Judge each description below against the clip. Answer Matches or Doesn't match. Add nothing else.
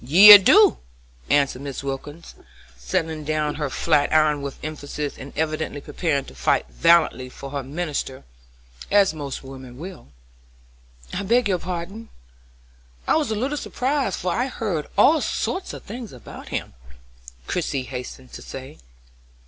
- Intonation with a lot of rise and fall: Matches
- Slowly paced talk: Doesn't match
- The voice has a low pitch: Doesn't match